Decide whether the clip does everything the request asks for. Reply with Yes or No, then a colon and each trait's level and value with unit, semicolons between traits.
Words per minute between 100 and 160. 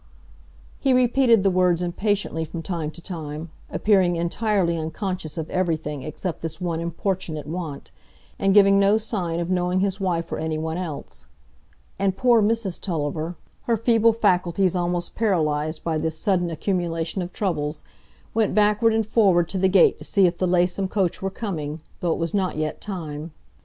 No: average, 170 wpm